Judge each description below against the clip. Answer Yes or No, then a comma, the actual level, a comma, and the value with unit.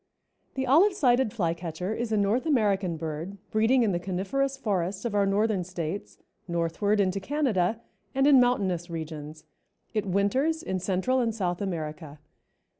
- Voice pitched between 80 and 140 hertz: No, high, 200 Hz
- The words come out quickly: No, average, 155 wpm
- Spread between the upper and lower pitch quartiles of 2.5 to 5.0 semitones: No, wide, 5.5 semitones